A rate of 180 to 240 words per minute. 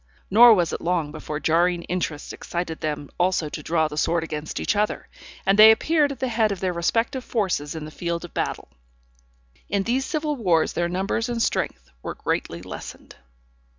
Yes: average, 185 wpm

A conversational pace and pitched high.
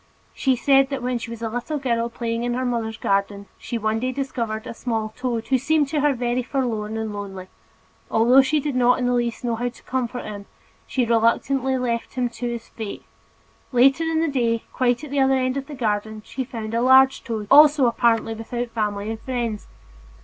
No: fast, 210 wpm; high, 240 Hz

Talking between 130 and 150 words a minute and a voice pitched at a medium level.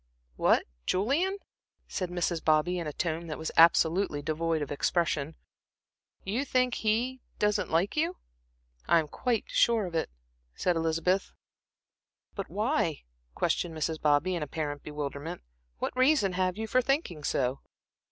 Yes: average, 140 wpm; medium, 175 Hz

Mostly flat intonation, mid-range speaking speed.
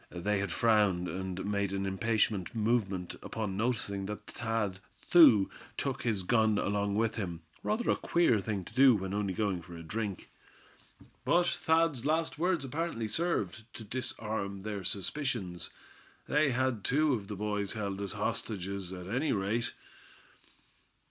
No: average, 3.8 semitones; average, 150 wpm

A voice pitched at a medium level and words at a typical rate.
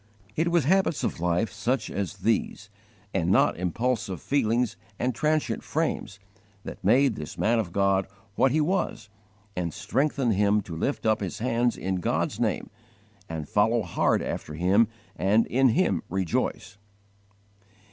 No: low, 110 Hz; average, 145 wpm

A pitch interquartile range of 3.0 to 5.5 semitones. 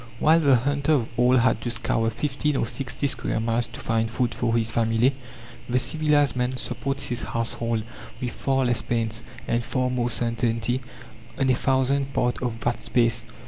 No: narrow, 2.6 semitones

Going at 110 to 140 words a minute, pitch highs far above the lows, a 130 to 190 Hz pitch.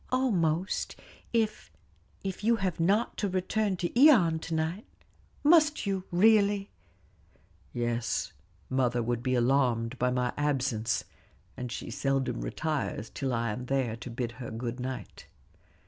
Yes: slow, 135 wpm; wide, 8.1 semitones; medium, 140 Hz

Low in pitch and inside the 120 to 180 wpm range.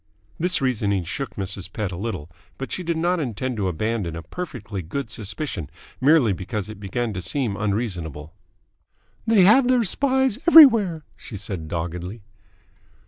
Yes: low, 110 Hz; average, 150 wpm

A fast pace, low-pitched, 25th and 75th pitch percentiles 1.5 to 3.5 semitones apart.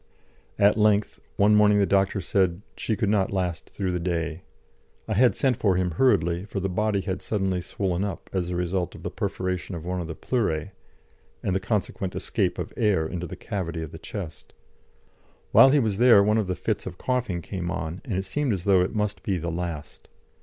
Yes: fast, 210 wpm; very low, 95 Hz; average, 2.9 semitones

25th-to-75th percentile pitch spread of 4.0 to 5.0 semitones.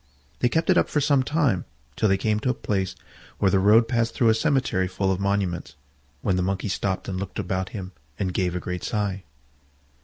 No: average, 3.6 semitones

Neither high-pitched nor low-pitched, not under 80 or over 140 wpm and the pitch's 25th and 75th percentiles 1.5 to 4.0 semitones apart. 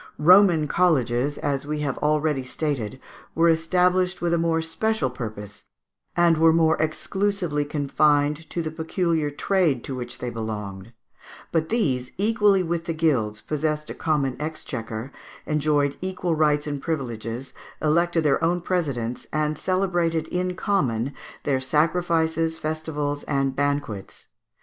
Yes: medium, 155 Hz; slow, 135 wpm; average, 3.7 semitones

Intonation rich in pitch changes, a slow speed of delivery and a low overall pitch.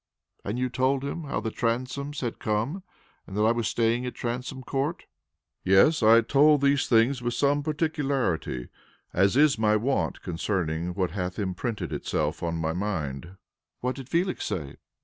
No: wide, 6.3 semitones; average, 165 wpm; low, 115 Hz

